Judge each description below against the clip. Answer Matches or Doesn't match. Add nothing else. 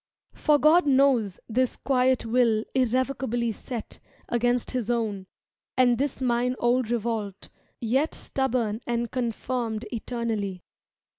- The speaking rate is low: Matches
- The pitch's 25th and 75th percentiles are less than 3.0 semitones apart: Matches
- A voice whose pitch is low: Doesn't match